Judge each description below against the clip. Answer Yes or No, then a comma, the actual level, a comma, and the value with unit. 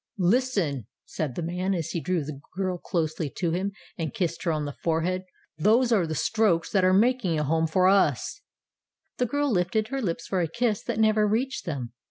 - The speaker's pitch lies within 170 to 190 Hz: Yes, medium, 185 Hz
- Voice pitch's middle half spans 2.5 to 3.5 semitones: No, average, 4.9 semitones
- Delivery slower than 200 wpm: No, fast, 205 wpm